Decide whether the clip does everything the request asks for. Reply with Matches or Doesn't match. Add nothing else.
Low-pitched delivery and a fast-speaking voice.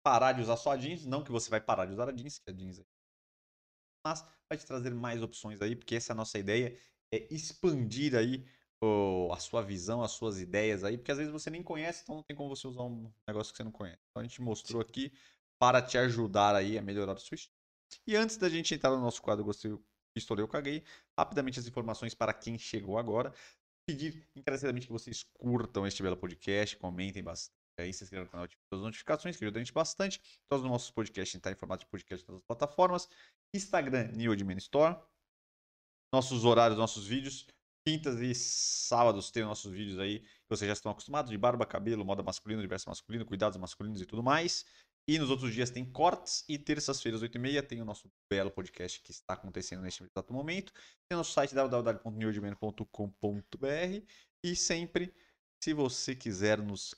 Matches